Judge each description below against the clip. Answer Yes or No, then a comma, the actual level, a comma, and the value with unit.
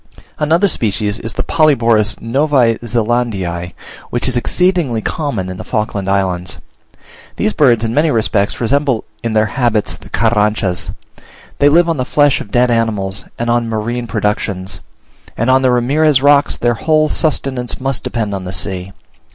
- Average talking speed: Yes, average, 160 wpm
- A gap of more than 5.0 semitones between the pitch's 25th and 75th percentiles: No, average, 4.5 semitones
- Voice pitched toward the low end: Yes, low, 115 Hz